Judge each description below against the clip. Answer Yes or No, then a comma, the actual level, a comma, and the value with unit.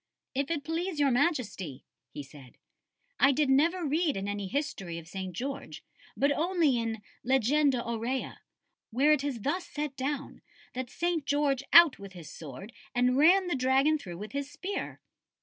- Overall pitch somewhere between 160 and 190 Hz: No, very high, 270 Hz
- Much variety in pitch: Yes, wide, 5.7 semitones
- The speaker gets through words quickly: No, average, 165 wpm